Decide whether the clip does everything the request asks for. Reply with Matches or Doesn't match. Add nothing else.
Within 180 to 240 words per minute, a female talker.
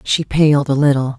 Matches